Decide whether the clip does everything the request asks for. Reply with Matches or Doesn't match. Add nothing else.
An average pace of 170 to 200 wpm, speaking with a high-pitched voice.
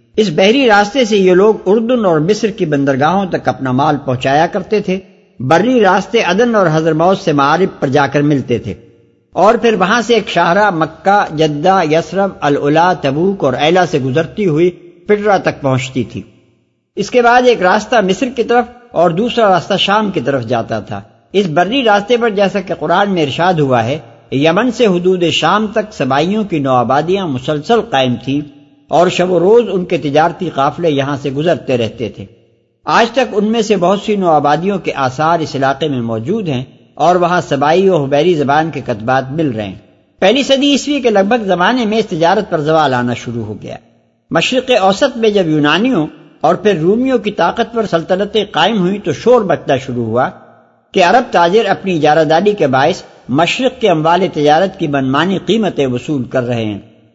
Doesn't match